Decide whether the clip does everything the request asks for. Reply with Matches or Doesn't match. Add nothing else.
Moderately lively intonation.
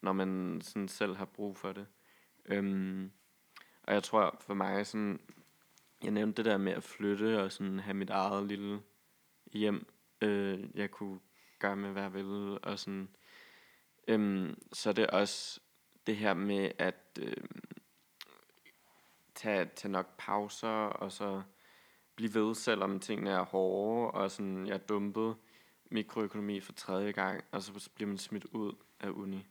Doesn't match